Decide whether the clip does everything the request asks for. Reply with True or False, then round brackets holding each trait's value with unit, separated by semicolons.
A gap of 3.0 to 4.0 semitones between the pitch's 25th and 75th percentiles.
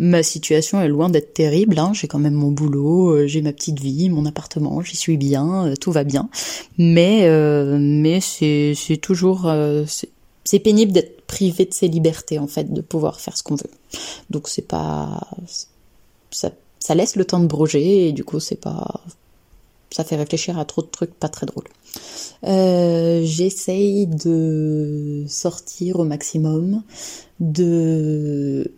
True (3.3 semitones)